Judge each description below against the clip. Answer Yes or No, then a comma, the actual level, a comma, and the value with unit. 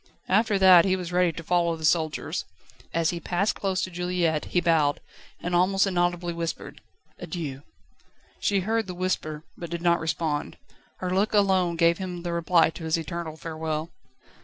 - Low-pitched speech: No, medium, 175 Hz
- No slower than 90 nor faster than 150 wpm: No, average, 170 wpm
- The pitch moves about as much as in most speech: No, narrow, 2.1 semitones